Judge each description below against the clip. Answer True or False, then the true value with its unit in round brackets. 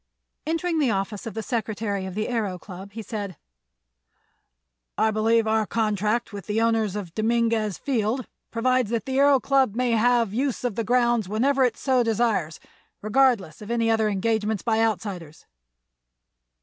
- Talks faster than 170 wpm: False (160 wpm)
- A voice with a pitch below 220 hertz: False (225 Hz)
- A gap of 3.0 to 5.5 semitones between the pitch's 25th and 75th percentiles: False (2.5 semitones)